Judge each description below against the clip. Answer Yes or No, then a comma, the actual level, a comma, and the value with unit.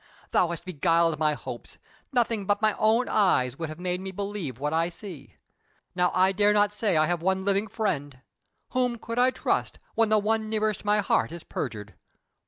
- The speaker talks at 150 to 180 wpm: No, average, 190 wpm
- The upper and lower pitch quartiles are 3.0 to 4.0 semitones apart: No, average, 4.5 semitones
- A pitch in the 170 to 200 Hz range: Yes, high, 190 Hz